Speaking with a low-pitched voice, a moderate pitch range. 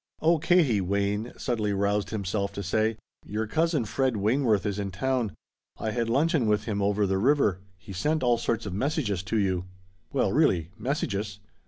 Yes: low, 105 Hz; average, 4.1 semitones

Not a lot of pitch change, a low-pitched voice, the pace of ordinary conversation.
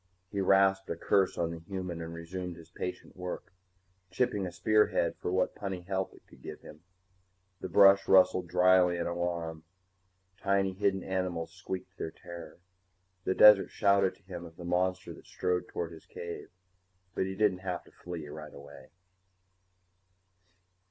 Yes: narrow, 1.9 semitones; very low, 90 Hz; average, 160 wpm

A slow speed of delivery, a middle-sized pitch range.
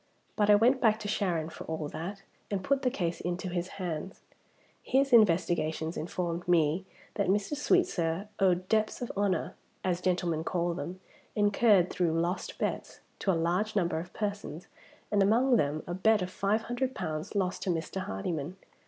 No: average, 170 wpm; average, 3.7 semitones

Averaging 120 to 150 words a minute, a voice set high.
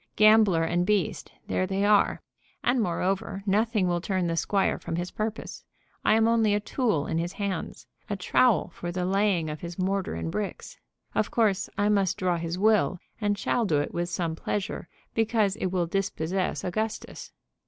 No: average, 180 wpm; high, 195 Hz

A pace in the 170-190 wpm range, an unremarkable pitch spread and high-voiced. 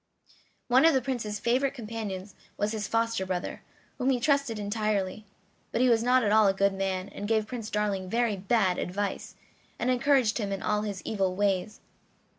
Yes: average, 185 wpm; average, 3.3 semitones; high, 215 Hz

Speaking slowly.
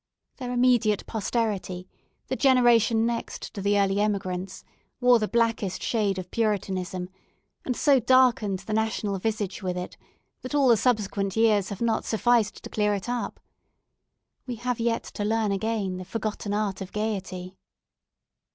No: average, 150 wpm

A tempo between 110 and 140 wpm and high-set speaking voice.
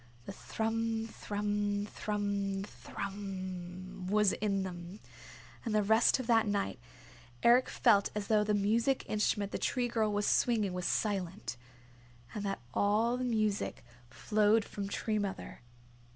Yes: slow, 135 wpm; high, 205 Hz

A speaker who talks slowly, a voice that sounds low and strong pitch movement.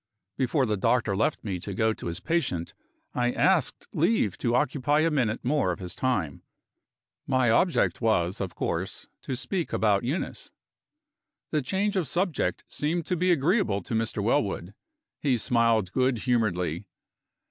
No: average, 155 wpm; low, 120 Hz; wide, 6.7 semitones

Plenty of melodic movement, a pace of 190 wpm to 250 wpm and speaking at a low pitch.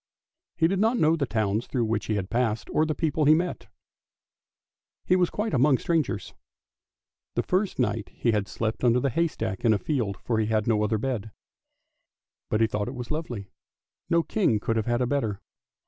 Yes: wide, 6.2 semitones; average, 195 wpm; low, 120 Hz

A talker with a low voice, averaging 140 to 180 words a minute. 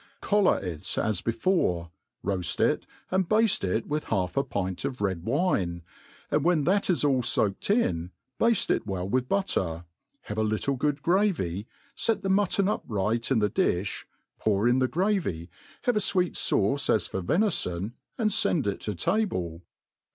Yes: low, 120 Hz; average, 165 wpm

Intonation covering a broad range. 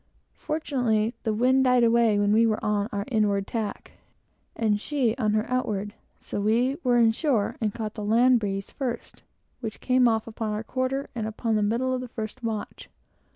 No: average, 3.0 semitones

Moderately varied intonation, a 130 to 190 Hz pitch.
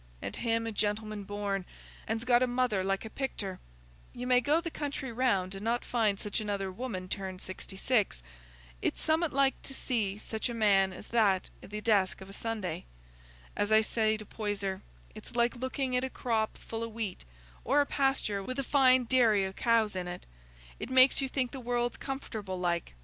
No: average, 4.3 semitones; high, 225 Hz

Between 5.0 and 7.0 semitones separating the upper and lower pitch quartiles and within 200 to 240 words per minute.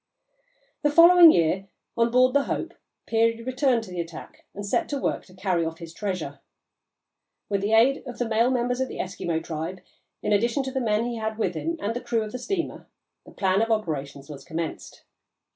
Yes: wide, 5.5 semitones; fast, 205 wpm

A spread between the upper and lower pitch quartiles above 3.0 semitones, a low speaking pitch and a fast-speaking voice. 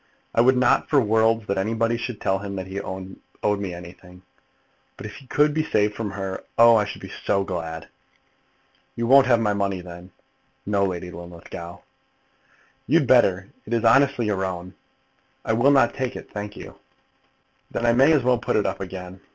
No: average, 4.0 semitones; low, 105 Hz; average, 190 wpm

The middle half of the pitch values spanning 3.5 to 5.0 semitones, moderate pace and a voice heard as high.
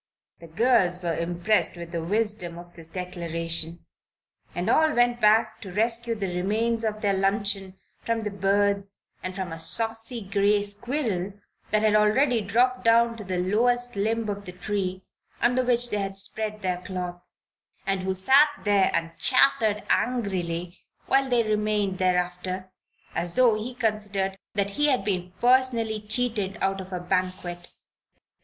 Yes: average, 3.8 semitones; average, 155 wpm; high, 205 Hz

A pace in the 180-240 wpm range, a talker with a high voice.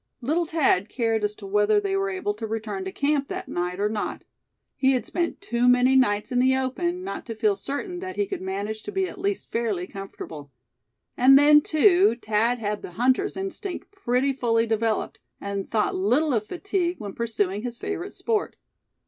Yes: average, 190 wpm; high, 245 Hz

